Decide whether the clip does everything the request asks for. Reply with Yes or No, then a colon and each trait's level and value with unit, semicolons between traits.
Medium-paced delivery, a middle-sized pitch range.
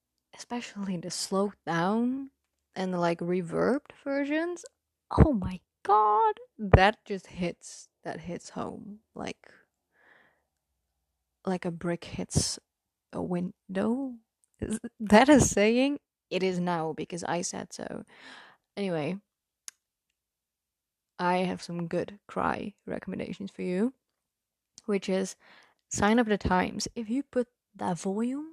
No: slow, 120 wpm; average, 4.8 semitones